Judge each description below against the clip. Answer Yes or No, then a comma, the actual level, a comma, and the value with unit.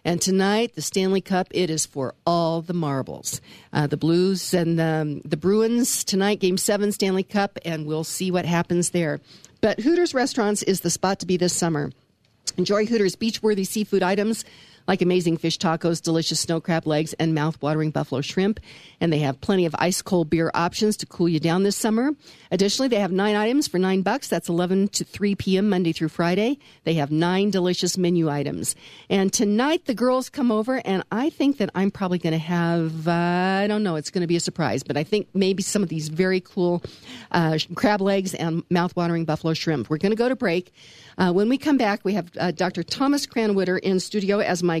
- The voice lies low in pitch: No, medium, 180 Hz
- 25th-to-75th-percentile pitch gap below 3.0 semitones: No, average, 3.6 semitones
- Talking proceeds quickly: Yes, fast, 210 wpm